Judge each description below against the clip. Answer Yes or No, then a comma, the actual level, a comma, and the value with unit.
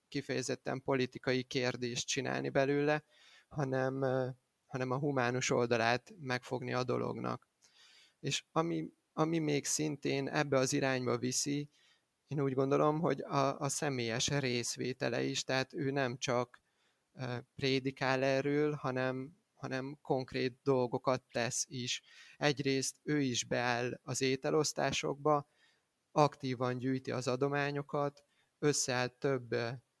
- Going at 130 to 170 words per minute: No, average, 110 wpm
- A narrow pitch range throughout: Yes, narrow, 2.2 semitones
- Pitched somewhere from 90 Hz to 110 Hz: No, low, 135 Hz